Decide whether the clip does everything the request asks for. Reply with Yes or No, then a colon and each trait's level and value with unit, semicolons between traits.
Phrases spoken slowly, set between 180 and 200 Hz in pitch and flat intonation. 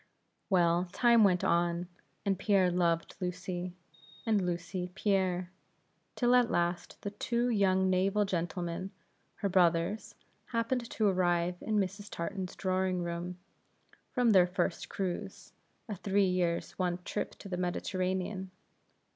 Yes: slow, 125 wpm; medium, 185 Hz; narrow, 2.3 semitones